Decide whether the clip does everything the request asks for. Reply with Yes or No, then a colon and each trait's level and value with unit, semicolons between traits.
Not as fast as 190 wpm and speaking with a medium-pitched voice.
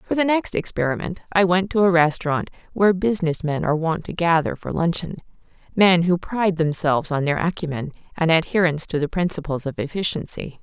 Yes: average, 180 wpm; medium, 170 Hz